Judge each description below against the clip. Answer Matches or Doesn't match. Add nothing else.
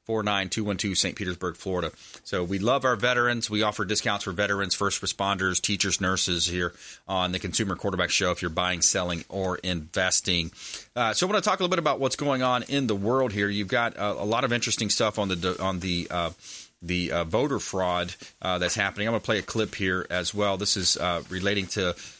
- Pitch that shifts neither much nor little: Matches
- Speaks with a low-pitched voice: Matches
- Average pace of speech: Doesn't match